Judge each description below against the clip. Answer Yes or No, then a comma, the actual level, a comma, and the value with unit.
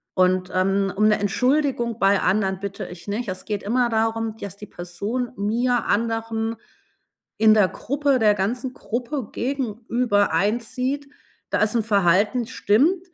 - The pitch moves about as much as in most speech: Yes, average, 3.5 semitones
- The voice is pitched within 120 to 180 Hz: No, high, 220 Hz